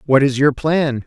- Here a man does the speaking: Yes, male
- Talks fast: Yes, fast, 225 wpm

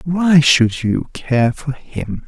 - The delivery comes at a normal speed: Yes, average, 160 wpm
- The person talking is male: Yes, male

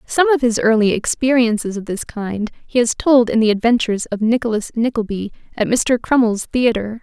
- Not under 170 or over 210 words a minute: Yes, average, 180 wpm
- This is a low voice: No, high, 230 Hz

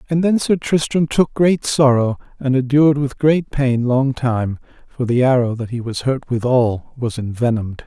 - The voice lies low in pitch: Yes, low, 130 Hz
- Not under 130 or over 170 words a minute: No, average, 185 wpm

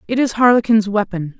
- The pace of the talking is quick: No, average, 175 wpm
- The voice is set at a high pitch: Yes, high, 215 Hz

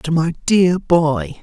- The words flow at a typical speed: Yes, average, 170 wpm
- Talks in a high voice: No, medium, 160 Hz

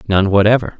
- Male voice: Yes, male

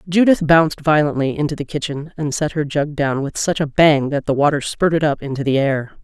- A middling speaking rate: No, fast, 230 wpm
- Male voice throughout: No, female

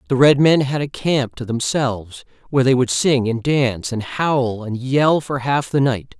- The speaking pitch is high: No, low, 130 Hz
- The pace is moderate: No, fast, 225 wpm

